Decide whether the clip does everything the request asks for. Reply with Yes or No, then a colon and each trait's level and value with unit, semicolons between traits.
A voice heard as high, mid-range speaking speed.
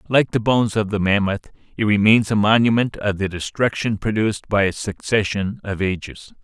No: low, 105 Hz; average, 175 wpm